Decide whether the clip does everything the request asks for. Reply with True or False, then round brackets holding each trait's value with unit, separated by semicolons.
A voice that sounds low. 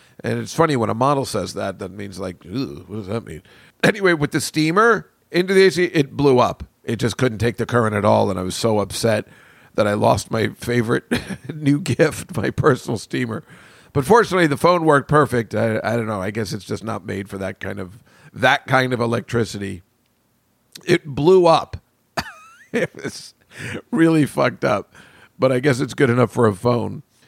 True (120 Hz)